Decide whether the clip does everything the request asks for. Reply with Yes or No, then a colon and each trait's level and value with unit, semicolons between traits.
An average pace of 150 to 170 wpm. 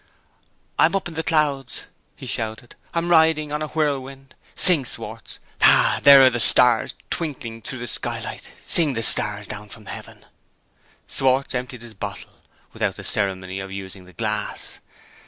Yes: average, 155 wpm